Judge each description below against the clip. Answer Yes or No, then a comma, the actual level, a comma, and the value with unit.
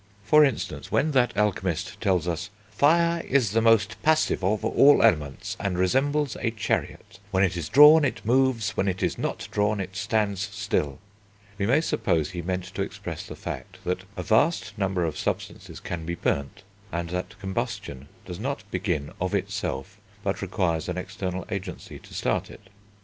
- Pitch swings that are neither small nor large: Yes, average, 4.1 semitones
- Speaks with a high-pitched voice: No, low, 100 Hz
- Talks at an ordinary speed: Yes, average, 175 wpm